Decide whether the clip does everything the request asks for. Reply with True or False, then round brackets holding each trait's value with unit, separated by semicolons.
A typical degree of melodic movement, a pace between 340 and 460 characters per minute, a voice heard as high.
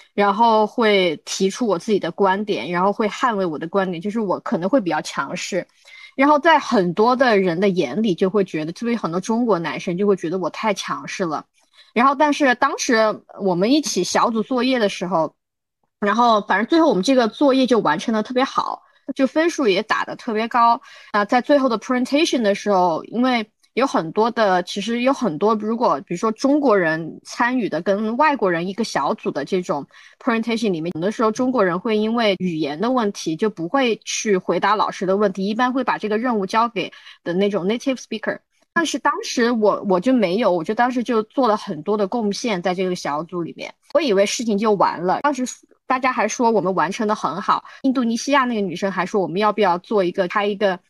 True (4.7 semitones; 350 characters per minute; 215 Hz)